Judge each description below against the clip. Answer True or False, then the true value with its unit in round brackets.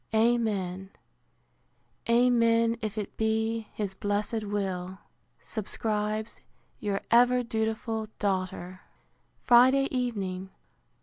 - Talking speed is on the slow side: True (80 wpm)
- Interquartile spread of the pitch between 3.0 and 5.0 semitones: False (2.6 semitones)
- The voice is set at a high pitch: True (220 Hz)